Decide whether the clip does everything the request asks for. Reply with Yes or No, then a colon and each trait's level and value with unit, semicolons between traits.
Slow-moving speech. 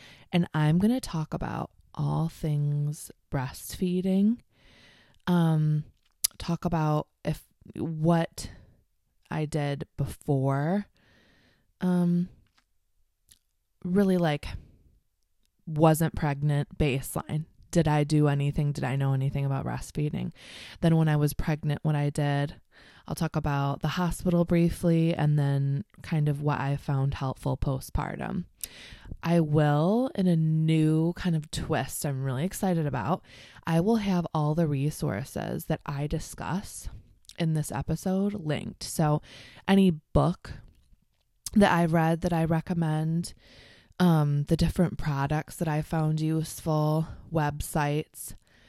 Yes: slow, 120 wpm